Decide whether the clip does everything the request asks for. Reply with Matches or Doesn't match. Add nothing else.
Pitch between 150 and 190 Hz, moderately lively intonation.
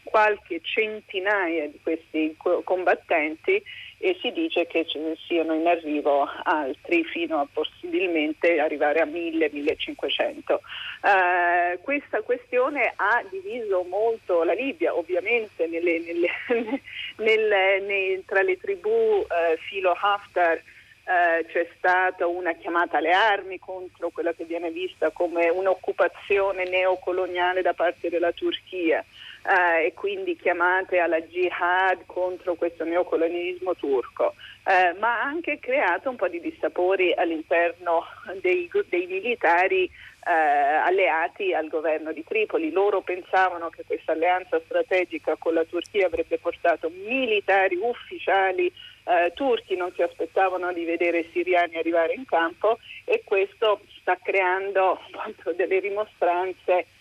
Doesn't match